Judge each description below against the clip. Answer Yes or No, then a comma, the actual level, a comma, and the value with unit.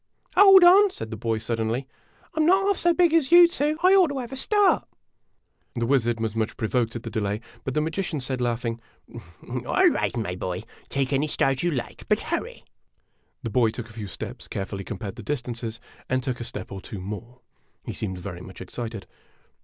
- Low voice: Yes, low, 120 Hz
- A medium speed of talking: No, fast, 210 wpm